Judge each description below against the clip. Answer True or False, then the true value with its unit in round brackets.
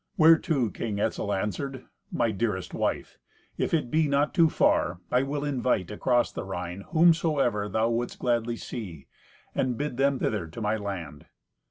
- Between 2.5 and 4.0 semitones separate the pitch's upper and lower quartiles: False (5.5 semitones)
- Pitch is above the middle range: False (120 Hz)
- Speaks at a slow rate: False (160 wpm)